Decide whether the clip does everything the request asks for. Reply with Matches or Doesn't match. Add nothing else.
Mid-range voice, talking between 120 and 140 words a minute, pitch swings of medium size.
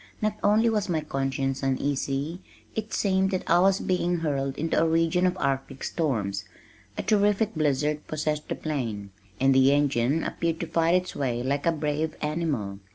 Doesn't match